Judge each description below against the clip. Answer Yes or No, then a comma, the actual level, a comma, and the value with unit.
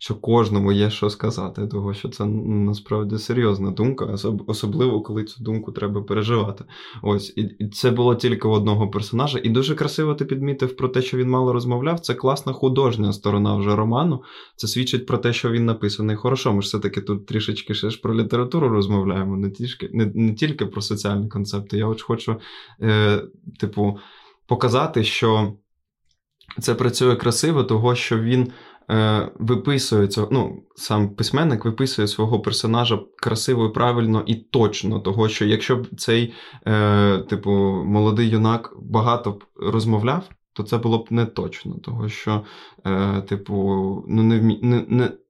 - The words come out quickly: Yes, fast, 160 wpm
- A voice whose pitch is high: No, low, 110 Hz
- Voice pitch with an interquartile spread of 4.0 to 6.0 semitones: No, average, 2.9 semitones